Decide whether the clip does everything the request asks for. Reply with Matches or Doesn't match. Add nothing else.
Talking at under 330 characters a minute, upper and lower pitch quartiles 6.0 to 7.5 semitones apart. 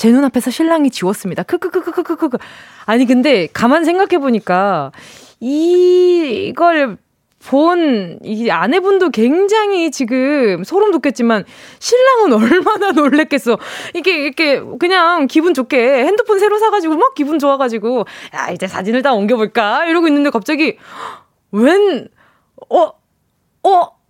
Matches